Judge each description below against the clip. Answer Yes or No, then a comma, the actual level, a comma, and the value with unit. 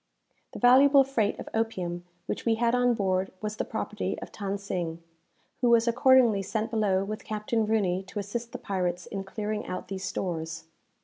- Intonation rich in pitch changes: No, average, 3.5 semitones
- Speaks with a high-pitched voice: Yes, high, 210 Hz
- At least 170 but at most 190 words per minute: Yes, average, 180 wpm